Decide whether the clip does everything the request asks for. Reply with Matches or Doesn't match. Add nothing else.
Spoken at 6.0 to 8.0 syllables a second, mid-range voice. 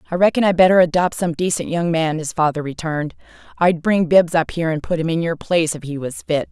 Matches